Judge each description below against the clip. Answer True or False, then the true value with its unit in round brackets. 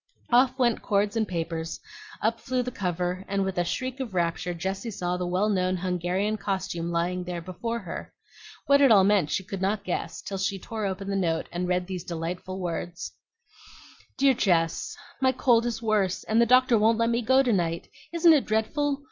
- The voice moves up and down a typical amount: True (4.5 semitones)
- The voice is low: False (195 Hz)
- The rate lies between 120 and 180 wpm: False (200 wpm)